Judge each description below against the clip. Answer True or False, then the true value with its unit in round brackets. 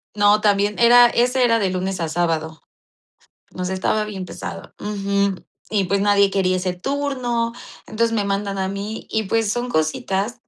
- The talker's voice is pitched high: True (200 Hz)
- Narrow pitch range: False (3.2 semitones)